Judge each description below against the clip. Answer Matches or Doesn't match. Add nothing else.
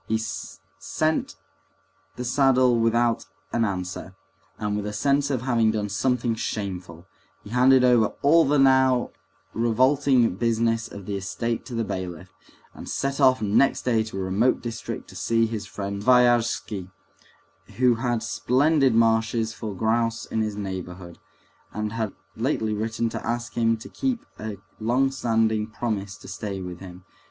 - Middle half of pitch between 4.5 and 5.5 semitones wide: Doesn't match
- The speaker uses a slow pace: Doesn't match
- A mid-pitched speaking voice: Doesn't match